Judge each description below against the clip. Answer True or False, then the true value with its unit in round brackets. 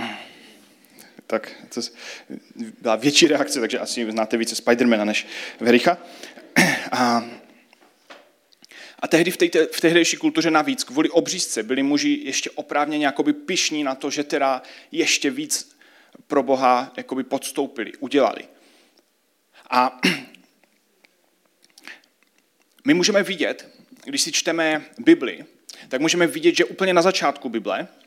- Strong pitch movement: True (6.9 semitones)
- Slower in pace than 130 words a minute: True (120 wpm)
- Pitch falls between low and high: True (160 Hz)